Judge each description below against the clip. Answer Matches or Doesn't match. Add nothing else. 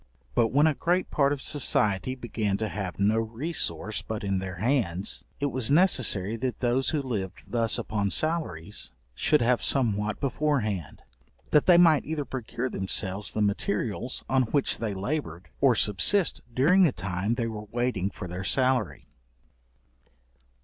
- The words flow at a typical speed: Matches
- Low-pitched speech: Matches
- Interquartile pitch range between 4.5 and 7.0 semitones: Matches